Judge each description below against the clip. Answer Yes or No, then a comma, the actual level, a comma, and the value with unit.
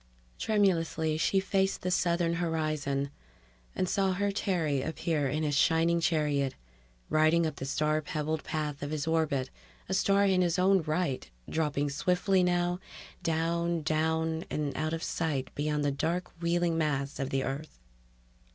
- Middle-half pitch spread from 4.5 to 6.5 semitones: No, average, 2.8 semitones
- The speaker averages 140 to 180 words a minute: Yes, average, 150 wpm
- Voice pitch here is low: No, medium, 160 Hz